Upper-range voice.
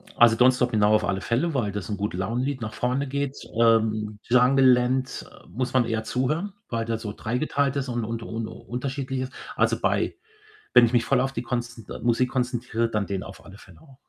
No: low, 120 Hz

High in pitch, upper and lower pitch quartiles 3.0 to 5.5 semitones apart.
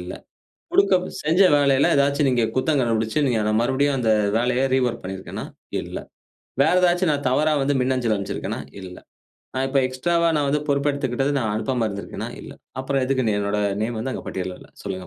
No: low, 130 Hz; average, 4.1 semitones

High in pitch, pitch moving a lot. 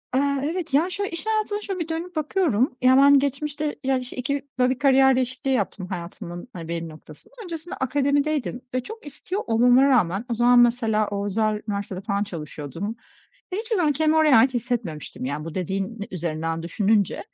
Yes: very high, 250 Hz; wide, 6.6 semitones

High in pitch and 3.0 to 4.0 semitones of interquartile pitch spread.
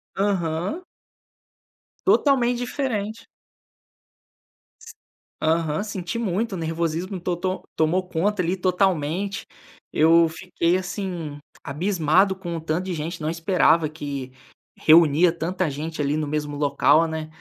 No: medium, 170 Hz; average, 3.4 semitones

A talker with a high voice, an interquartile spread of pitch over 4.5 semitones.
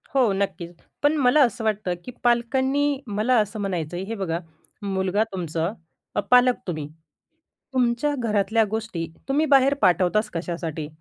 Yes: high, 215 Hz; wide, 5.6 semitones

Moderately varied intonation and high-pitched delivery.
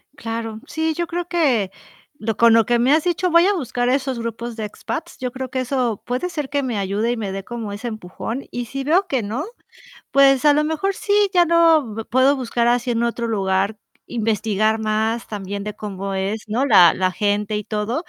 Yes: average, 4.8 semitones; high, 235 Hz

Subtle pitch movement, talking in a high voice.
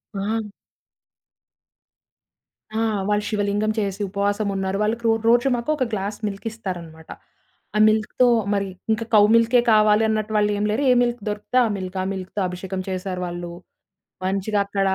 Yes: narrow, 2.2 semitones; high, 205 Hz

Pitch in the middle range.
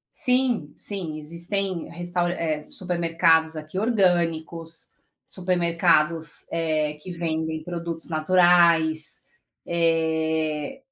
Yes: medium, 165 Hz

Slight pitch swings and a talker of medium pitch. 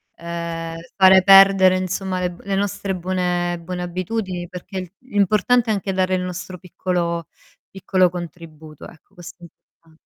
Yes: narrow, 1.8 semitones; medium, 180 Hz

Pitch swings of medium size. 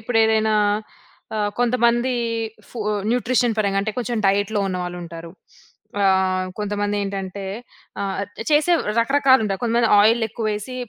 Yes: average, 3.2 semitones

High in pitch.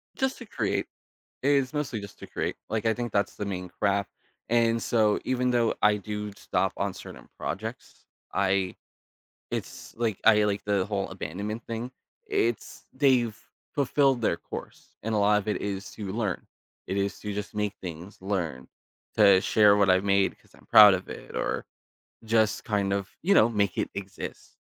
No: low, 105 Hz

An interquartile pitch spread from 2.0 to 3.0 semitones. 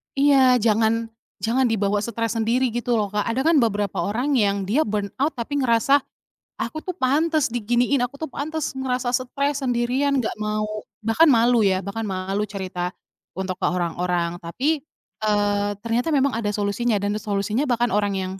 No: average, 4.2 semitones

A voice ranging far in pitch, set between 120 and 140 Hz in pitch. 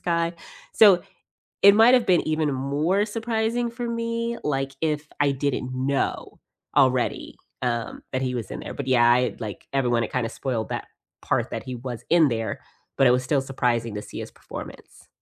Yes: wide, 6.6 semitones; low, 135 Hz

